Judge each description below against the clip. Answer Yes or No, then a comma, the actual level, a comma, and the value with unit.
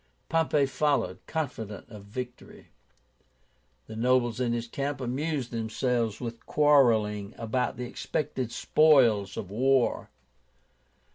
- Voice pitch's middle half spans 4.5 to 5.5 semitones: No, average, 3.5 semitones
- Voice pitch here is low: Yes, low, 125 Hz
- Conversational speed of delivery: No, slow, 110 wpm